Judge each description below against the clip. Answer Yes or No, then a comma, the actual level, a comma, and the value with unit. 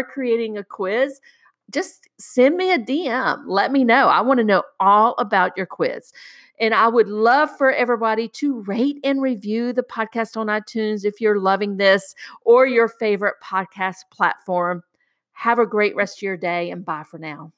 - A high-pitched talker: Yes, high, 225 Hz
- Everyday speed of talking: Yes, average, 180 wpm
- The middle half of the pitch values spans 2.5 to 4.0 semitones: No, average, 4.6 semitones